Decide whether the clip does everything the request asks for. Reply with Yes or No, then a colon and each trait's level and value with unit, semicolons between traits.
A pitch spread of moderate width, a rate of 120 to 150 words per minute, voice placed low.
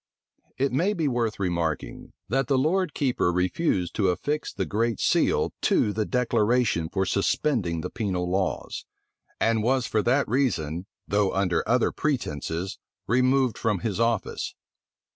No: wide, 5.7 semitones; average, 145 wpm; low, 110 Hz